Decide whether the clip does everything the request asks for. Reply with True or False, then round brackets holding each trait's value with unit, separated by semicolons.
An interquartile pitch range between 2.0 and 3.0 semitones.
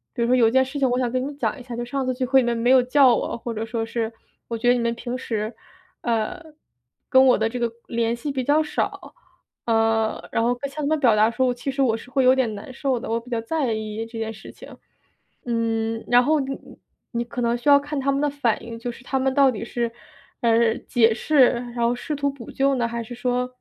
True (2.6 semitones)